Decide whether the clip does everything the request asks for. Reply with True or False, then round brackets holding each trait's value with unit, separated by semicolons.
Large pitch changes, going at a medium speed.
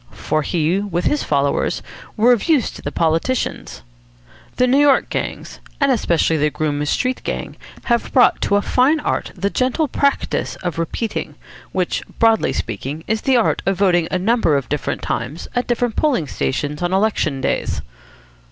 True (8.0 semitones; 170 wpm)